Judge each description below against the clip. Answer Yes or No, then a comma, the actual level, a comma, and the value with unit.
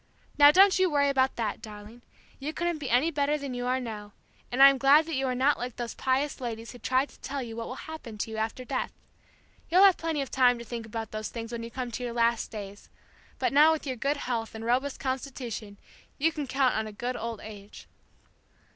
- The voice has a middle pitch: No, very high, 255 Hz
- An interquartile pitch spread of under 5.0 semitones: Yes, average, 3.6 semitones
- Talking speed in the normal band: No, fast, 235 wpm